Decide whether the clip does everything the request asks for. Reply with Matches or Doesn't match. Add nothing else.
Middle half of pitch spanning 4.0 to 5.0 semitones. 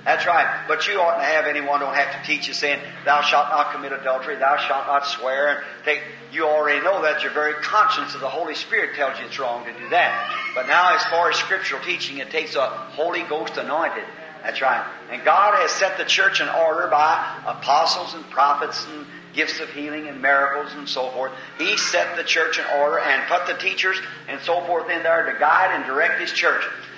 Doesn't match